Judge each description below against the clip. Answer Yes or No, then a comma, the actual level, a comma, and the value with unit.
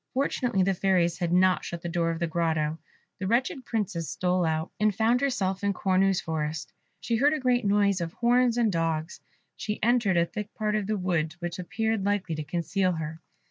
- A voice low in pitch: No, high, 190 Hz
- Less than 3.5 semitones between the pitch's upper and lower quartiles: No, average, 4.3 semitones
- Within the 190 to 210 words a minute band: Yes, average, 200 wpm